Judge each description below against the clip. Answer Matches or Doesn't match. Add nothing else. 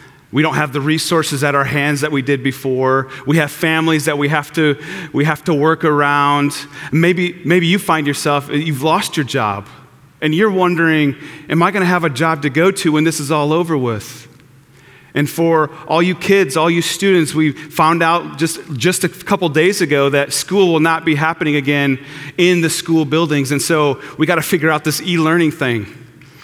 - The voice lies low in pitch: Doesn't match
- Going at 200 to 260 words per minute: Matches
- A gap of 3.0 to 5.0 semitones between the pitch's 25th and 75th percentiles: Doesn't match